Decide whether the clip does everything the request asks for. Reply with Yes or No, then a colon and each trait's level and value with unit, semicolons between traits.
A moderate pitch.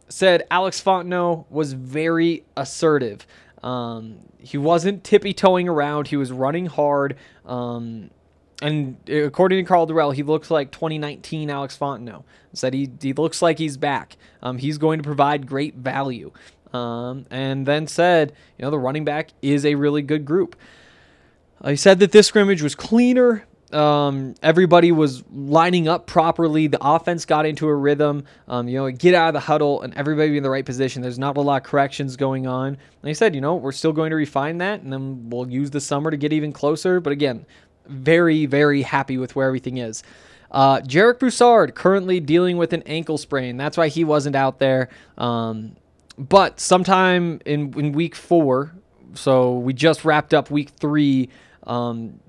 Yes: medium, 150 Hz